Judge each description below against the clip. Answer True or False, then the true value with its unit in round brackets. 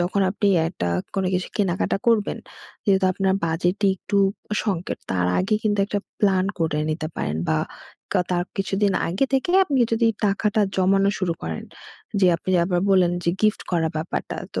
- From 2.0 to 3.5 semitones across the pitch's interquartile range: True (2.9 semitones)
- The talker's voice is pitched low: False (190 Hz)